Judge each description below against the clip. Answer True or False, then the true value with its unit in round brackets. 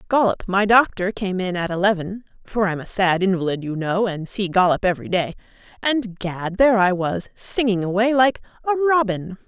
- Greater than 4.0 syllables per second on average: False (3.5 syllables/s)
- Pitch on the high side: True (200 Hz)